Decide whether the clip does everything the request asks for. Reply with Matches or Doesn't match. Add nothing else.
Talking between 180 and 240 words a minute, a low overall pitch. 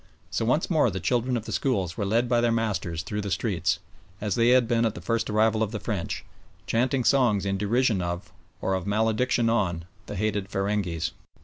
Matches